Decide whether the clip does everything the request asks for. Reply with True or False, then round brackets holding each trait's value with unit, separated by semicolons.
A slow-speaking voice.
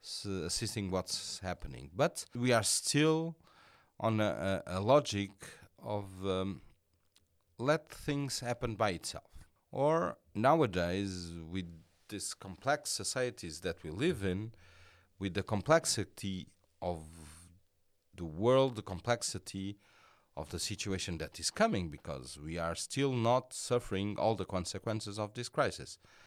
True (125 wpm)